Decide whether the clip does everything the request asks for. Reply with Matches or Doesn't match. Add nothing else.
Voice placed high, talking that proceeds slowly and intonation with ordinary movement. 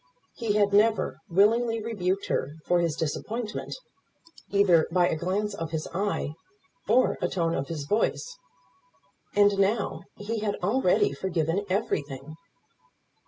Matches